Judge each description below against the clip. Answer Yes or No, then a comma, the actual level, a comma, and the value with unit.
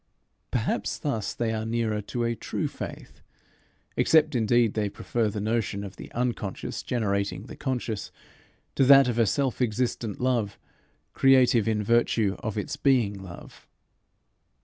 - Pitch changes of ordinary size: Yes, average, 3.0 semitones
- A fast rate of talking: No, average, 145 wpm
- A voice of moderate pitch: No, low, 115 Hz